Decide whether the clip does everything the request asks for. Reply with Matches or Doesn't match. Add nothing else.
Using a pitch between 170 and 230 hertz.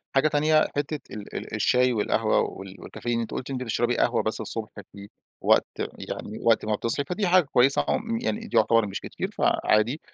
Doesn't match